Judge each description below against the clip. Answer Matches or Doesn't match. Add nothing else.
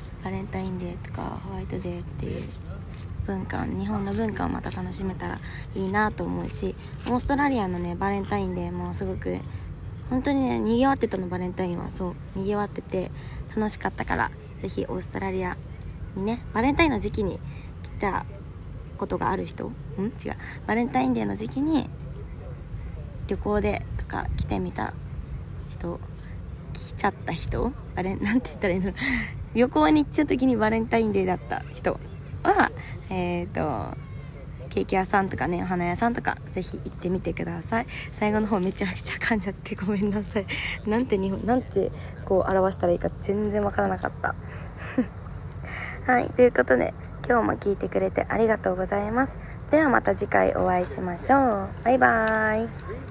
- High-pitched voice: Doesn't match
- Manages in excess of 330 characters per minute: Matches